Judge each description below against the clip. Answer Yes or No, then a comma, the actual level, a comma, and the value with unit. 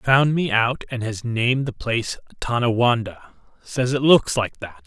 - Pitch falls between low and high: No, low, 120 Hz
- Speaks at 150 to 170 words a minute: Yes, average, 160 wpm